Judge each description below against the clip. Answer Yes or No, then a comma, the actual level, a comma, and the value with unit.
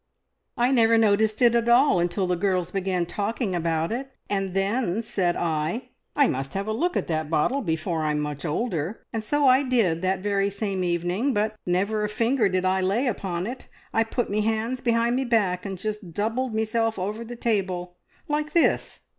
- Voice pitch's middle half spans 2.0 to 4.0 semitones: No, average, 4.5 semitones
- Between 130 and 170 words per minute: No, average, 195 wpm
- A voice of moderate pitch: No, high, 205 Hz